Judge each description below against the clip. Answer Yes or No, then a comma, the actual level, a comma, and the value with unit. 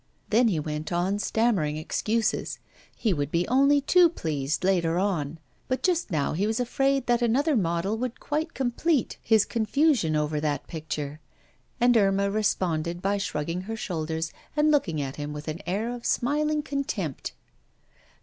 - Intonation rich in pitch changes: Yes, wide, 7.6 semitones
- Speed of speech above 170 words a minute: No, average, 160 wpm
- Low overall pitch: No, high, 200 Hz